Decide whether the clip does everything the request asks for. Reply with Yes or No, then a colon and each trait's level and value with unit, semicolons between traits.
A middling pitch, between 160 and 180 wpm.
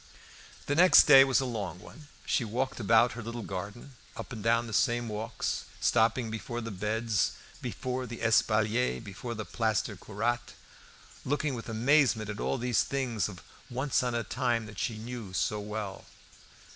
No: low, 115 Hz; average, 170 wpm